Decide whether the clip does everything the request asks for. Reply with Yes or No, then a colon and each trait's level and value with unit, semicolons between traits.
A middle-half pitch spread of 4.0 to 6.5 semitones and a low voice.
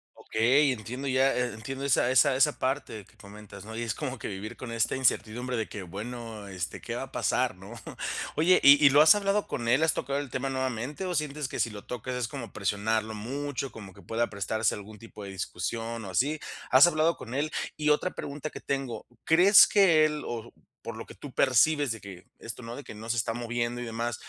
Yes: average, 4.3 semitones; low, 120 Hz